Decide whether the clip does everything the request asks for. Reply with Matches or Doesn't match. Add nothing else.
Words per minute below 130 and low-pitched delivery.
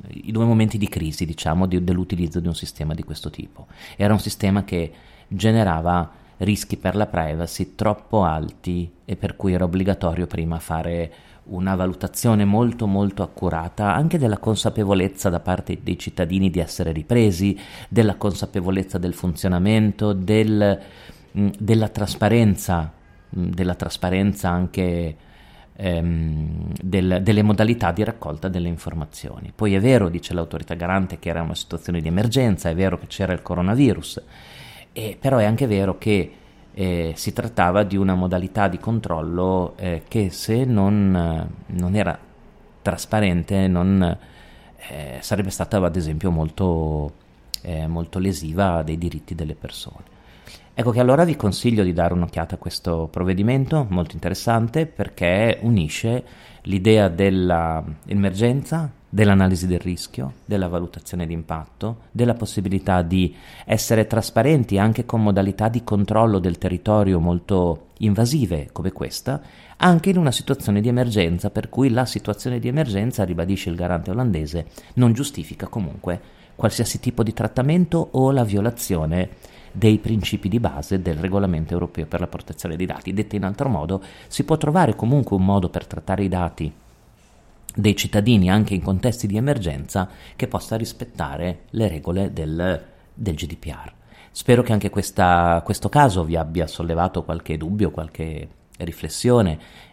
Doesn't match